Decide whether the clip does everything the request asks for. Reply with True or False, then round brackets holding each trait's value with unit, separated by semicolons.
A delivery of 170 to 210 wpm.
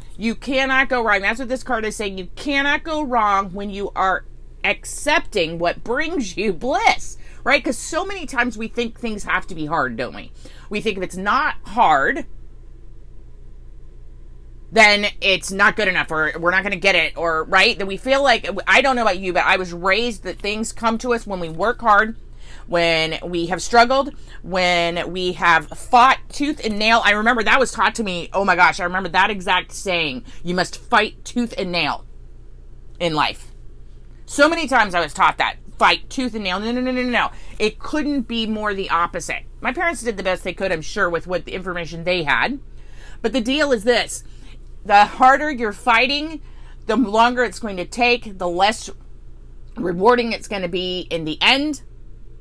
True (200 wpm)